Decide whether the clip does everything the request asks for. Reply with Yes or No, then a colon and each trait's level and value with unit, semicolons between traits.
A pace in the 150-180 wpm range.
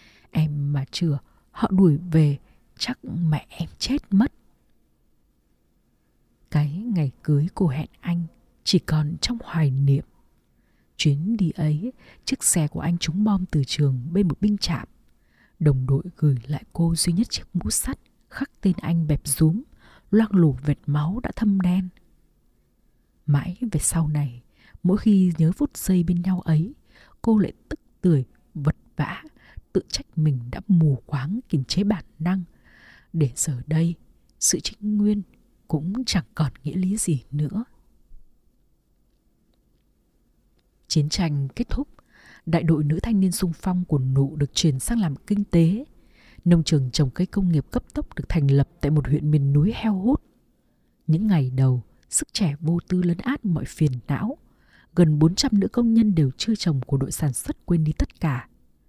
Yes: average, 170 wpm